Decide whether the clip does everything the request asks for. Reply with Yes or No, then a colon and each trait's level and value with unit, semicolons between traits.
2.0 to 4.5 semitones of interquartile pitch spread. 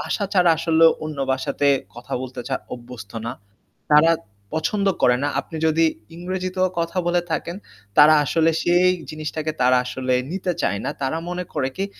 No: average, 5.0 semitones